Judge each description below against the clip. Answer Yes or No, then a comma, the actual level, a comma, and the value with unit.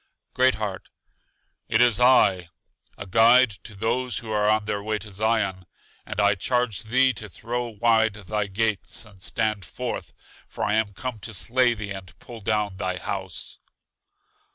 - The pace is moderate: Yes, average, 165 wpm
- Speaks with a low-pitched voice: Yes, low, 110 Hz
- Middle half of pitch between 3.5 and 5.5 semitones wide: No, average, 2.7 semitones